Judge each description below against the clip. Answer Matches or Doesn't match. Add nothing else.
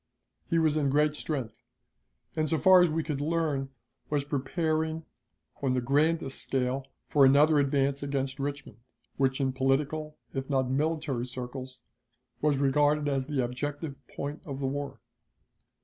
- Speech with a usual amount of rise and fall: Doesn't match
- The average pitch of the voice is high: Doesn't match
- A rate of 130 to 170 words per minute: Matches